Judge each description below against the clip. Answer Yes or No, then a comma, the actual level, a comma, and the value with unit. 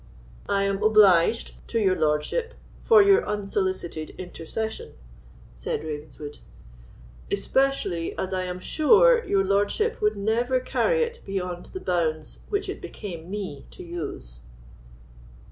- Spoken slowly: Yes, slow, 125 wpm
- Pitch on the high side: Yes, high, 195 Hz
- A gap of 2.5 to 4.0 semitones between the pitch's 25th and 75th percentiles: No, wide, 5.4 semitones